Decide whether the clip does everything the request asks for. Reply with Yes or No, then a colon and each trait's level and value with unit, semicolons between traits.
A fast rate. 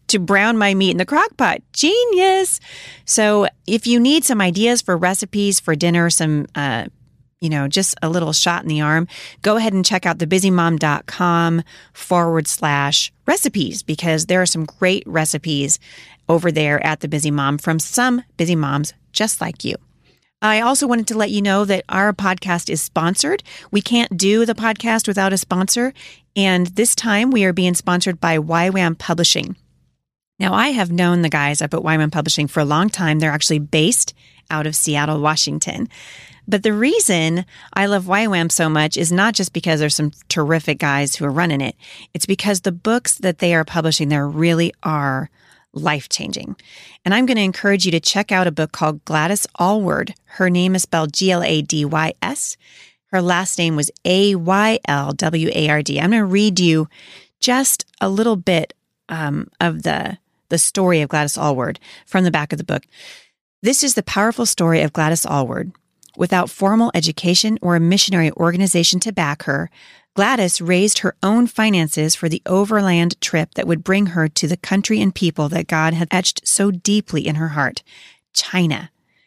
No: average, 185 wpm